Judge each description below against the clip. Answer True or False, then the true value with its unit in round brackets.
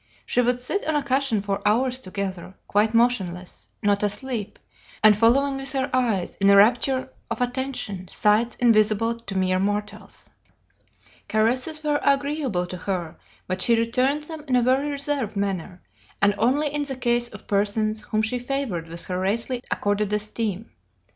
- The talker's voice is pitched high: True (230 Hz)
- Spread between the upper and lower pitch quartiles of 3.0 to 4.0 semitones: False (4.5 semitones)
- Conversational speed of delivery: True (160 wpm)